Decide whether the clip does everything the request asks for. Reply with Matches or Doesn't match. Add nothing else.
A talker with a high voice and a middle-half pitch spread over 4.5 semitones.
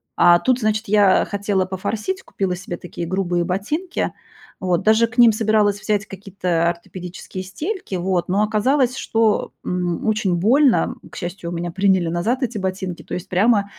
Doesn't match